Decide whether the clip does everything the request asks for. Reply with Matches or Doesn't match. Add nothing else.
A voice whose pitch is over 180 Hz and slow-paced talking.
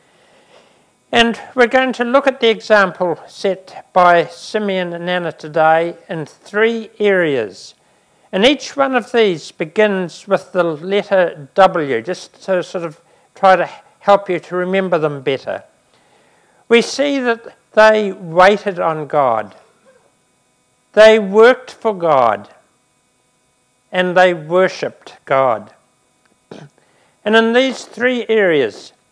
Matches